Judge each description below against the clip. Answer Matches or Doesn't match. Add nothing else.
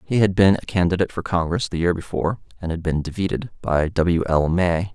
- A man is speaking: Matches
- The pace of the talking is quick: Matches